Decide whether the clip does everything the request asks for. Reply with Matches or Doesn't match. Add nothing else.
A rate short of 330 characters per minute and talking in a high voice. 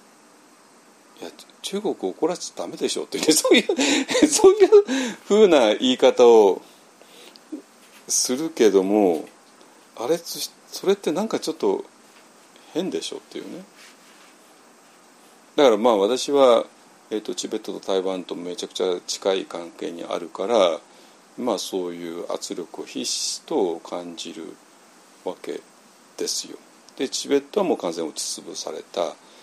Matches